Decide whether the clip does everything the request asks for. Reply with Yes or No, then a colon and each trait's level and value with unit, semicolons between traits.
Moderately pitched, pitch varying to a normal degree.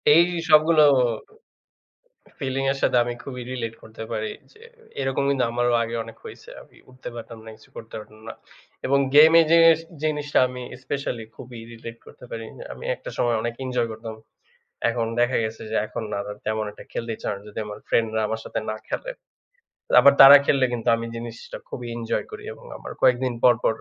No: low, 120 Hz; average, 3.2 semitones